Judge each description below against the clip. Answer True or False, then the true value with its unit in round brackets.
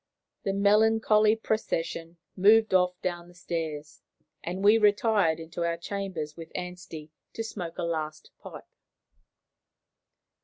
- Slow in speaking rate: True (120 wpm)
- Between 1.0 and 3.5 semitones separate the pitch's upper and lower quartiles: False (3.9 semitones)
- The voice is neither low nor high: True (180 Hz)